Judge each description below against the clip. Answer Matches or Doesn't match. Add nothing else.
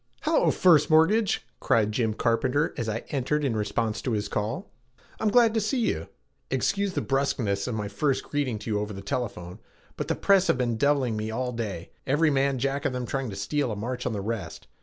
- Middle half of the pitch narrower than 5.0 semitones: Doesn't match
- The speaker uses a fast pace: Matches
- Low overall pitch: Matches